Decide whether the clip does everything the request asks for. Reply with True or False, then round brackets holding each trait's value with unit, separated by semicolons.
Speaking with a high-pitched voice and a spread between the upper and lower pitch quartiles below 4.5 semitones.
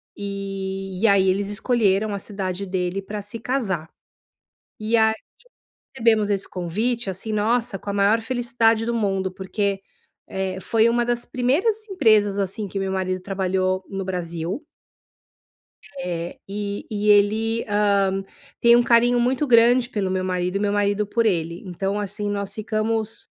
True (205 Hz; 2.9 semitones)